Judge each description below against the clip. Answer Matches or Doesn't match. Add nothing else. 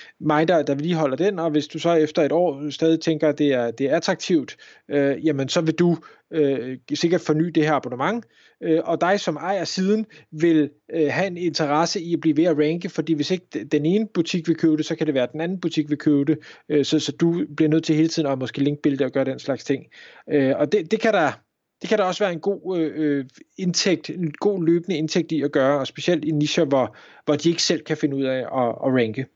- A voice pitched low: Doesn't match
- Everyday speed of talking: Doesn't match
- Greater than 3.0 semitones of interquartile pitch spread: Doesn't match